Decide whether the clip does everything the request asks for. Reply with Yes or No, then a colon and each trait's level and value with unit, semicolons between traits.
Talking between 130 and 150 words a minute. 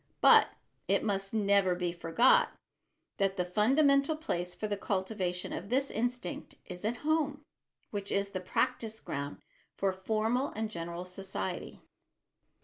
Yes: average, 140 wpm